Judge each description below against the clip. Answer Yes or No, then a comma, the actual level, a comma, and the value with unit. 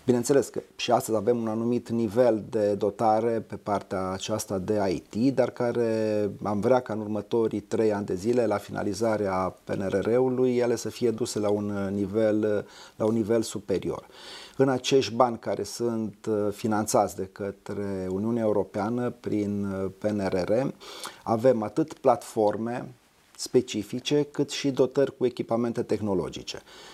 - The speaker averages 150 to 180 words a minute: No, average, 140 wpm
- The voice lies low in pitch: Yes, low, 110 Hz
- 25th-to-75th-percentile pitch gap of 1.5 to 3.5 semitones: Yes, average, 2.8 semitones